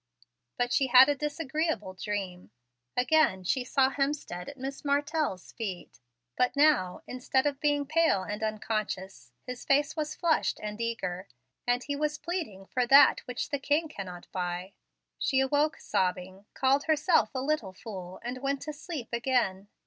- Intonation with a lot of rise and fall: Yes, wide, 6.8 semitones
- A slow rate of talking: No, average, 155 wpm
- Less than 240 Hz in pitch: No, very high, 255 Hz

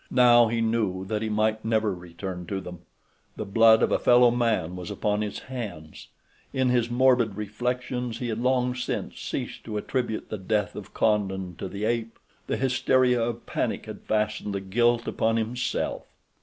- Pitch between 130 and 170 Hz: No, low, 110 Hz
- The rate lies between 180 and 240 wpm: No, average, 170 wpm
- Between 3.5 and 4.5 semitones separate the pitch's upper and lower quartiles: No, average, 3.0 semitones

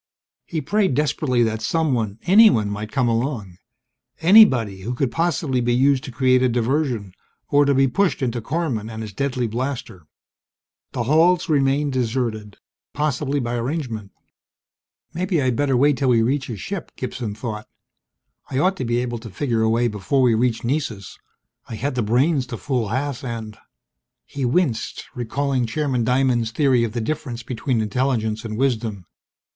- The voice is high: No, low, 125 Hz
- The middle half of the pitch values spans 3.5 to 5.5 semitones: Yes, average, 3.8 semitones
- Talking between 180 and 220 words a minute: No, average, 165 wpm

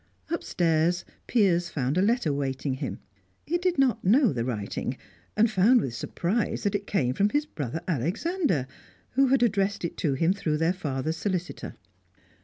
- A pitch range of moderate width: No, wide, 7.2 semitones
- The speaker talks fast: No, average, 165 wpm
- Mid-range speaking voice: Yes, medium, 180 Hz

